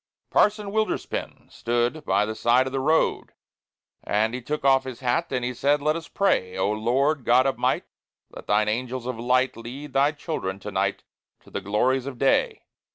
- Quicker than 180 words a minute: Yes, average, 190 wpm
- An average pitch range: Yes, average, 3.6 semitones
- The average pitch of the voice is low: Yes, low, 130 Hz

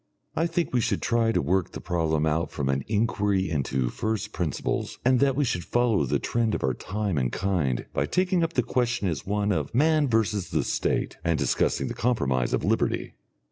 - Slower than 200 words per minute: No, fast, 205 wpm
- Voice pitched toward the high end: No, low, 100 Hz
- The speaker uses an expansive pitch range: Yes, wide, 7.5 semitones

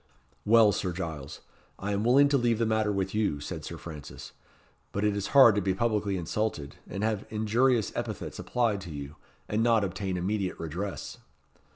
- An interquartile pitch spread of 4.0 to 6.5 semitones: No, average, 3.4 semitones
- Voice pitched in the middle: No, low, 100 Hz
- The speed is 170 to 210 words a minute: Yes, average, 180 wpm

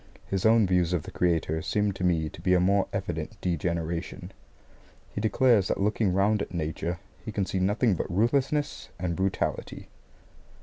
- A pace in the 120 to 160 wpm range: No, average, 170 wpm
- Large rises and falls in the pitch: No, average, 3.2 semitones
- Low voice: Yes, very low, 95 Hz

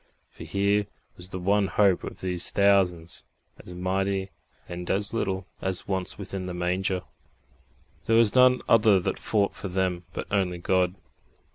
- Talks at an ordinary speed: Yes, average, 155 wpm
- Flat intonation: Yes, narrow, 1.8 semitones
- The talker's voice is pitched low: Yes, very low, 95 Hz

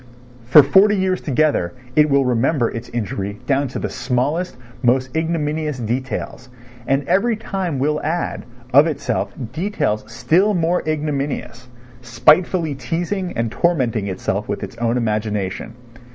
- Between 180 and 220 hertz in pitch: No, medium, 140 Hz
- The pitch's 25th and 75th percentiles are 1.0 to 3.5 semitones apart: No, wide, 5.4 semitones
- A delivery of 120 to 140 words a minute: Yes, slow, 135 wpm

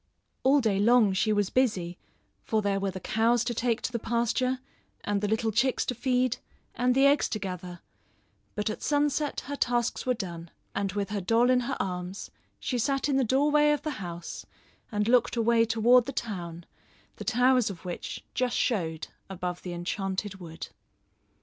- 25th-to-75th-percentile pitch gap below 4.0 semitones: No, average, 4.5 semitones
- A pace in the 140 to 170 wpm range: No, average, 180 wpm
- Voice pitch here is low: No, high, 225 Hz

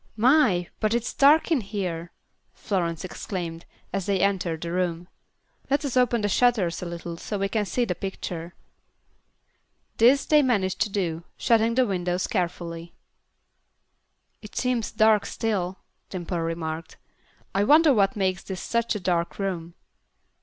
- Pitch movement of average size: Yes, average, 4.7 semitones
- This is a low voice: No, high, 195 Hz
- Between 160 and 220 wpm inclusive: No, average, 145 wpm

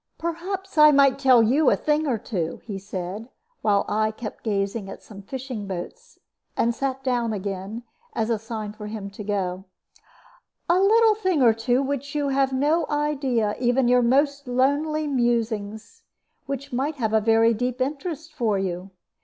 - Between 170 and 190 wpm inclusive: Yes, average, 175 wpm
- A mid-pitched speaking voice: No, high, 245 Hz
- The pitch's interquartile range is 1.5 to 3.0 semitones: No, average, 4.9 semitones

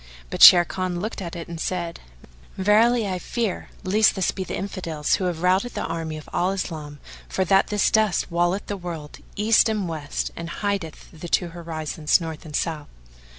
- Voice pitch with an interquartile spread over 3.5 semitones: No, average, 3.1 semitones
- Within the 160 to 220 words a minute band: Yes, average, 185 wpm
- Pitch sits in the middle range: Yes, medium, 175 Hz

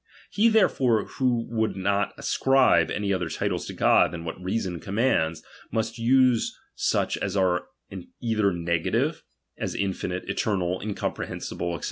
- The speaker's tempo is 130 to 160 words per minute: Yes, average, 140 wpm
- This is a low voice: Yes, low, 100 Hz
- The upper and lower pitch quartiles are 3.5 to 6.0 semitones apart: Yes, average, 4.5 semitones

